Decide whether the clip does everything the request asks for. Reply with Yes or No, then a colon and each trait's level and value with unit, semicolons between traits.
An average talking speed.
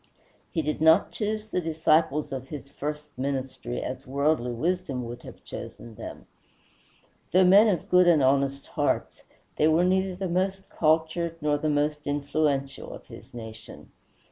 Yes: average, 155 wpm